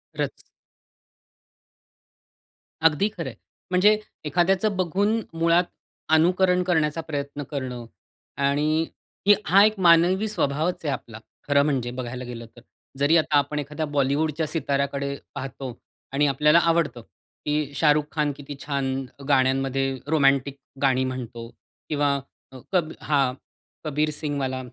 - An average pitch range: Yes, average, 3.3 semitones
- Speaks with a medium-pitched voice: Yes, medium, 145 Hz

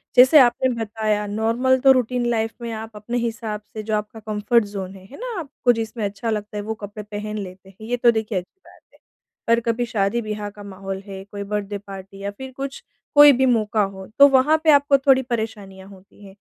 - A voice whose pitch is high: Yes, high, 220 Hz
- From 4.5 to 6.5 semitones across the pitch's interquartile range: No, average, 3.1 semitones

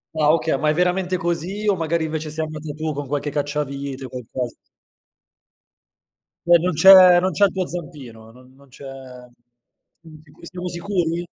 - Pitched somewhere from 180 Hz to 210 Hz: No, medium, 155 Hz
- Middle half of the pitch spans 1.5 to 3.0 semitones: No, average, 4.1 semitones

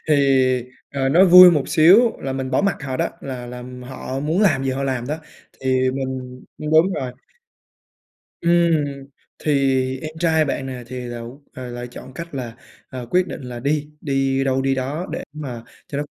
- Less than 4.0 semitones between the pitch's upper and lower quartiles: Yes, average, 3.3 semitones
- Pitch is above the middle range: No, low, 135 Hz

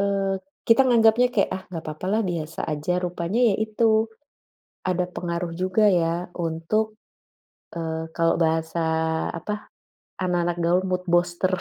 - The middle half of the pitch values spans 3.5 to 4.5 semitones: Yes, average, 3.8 semitones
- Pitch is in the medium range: Yes, medium, 180 Hz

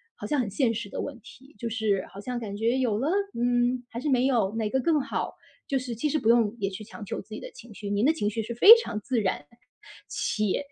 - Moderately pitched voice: No, high, 235 Hz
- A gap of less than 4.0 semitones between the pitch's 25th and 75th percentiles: Yes, average, 3.6 semitones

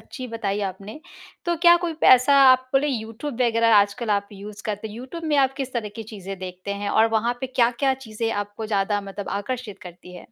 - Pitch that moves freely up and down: No, average, 4.1 semitones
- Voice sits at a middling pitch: No, high, 225 Hz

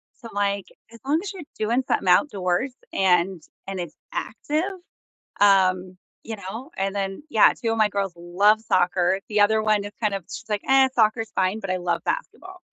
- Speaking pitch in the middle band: No, high, 205 Hz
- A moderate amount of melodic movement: Yes, average, 3.4 semitones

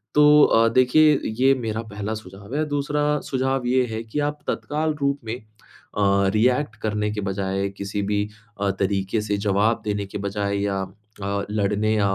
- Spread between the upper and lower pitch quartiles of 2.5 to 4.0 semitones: No, average, 4.5 semitones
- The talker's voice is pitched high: No, low, 110 Hz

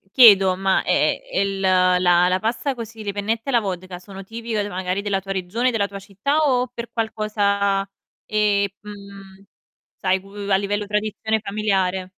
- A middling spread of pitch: No, narrow, 2.3 semitones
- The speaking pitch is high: Yes, high, 200 Hz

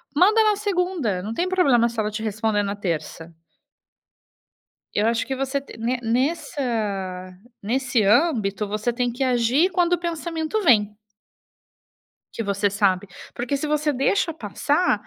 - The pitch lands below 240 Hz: No, high, 245 Hz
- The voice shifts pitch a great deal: Yes, wide, 7.3 semitones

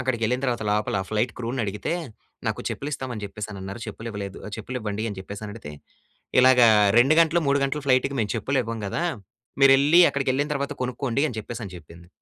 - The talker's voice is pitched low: Yes, low, 120 Hz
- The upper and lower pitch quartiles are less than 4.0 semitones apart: No, average, 4.5 semitones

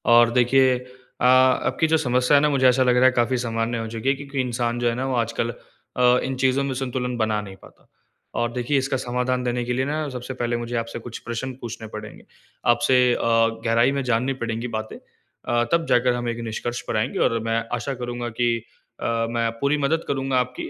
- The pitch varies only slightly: Yes, narrow, 1.9 semitones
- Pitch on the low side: Yes, low, 125 Hz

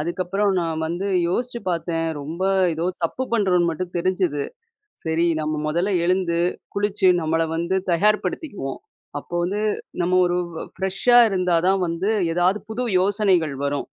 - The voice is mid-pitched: Yes, medium, 180 Hz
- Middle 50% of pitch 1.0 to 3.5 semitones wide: Yes, average, 2.9 semitones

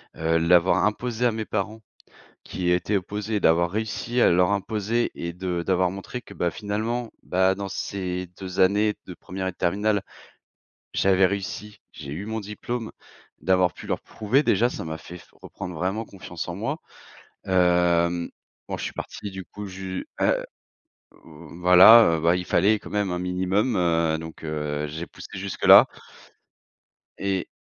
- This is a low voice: Yes, very low, 95 Hz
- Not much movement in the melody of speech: No, average, 3.1 semitones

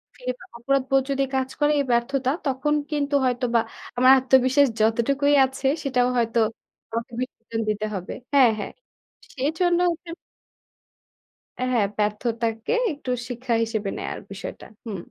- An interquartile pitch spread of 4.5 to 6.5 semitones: No, average, 3.1 semitones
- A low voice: No, very high, 255 Hz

